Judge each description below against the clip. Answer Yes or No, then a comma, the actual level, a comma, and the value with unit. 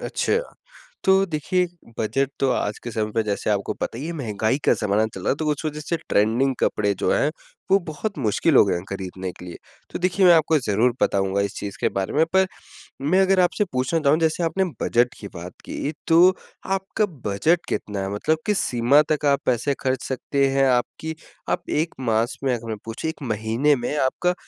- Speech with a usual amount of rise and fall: No, wide, 7.1 semitones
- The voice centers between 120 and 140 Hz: Yes, low, 135 Hz